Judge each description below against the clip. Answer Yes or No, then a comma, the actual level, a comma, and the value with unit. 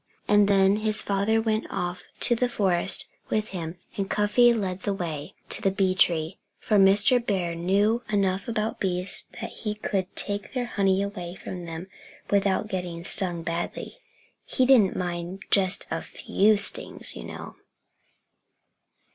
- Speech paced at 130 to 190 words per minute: Yes, average, 155 wpm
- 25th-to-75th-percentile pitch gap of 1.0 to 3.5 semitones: Yes, average, 2.8 semitones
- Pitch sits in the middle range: No, high, 195 Hz